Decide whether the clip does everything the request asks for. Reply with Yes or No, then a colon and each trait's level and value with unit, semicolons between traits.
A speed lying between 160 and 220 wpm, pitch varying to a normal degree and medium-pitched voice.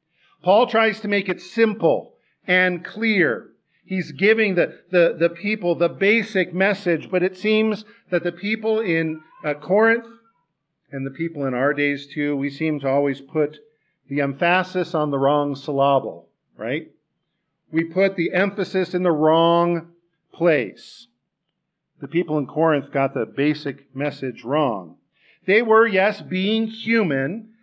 No: average, 145 wpm; average, 4.8 semitones; medium, 170 Hz